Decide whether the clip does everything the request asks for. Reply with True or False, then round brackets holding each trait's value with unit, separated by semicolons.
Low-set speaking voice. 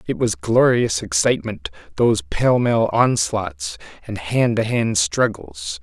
True (115 Hz)